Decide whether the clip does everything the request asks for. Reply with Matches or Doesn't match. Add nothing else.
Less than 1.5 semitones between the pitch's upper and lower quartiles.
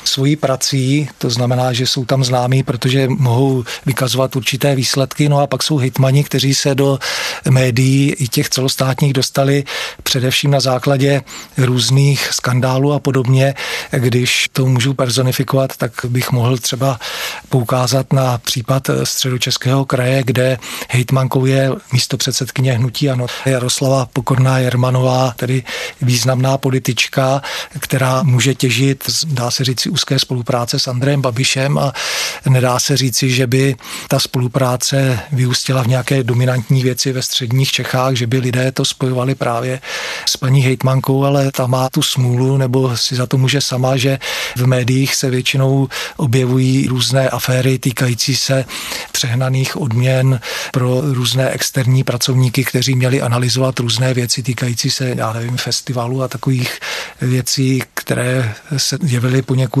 Matches